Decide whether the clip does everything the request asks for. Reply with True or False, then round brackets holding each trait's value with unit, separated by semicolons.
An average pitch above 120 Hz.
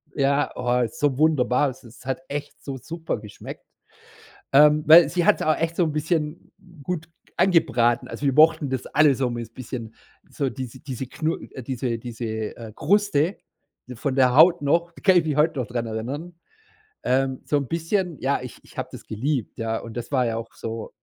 True (140 Hz)